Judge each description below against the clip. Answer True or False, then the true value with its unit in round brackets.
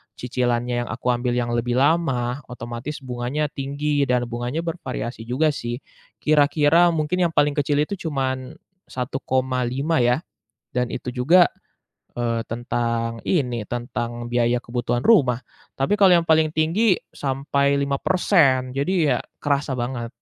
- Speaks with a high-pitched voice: False (130 Hz)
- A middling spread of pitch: True (3.7 semitones)